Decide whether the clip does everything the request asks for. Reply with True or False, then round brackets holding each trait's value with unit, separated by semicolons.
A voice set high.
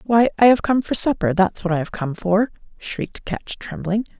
True (205 Hz)